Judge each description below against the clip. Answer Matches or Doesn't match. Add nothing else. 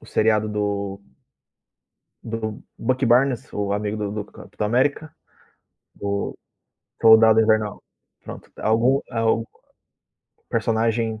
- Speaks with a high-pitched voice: Doesn't match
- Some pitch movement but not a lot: Doesn't match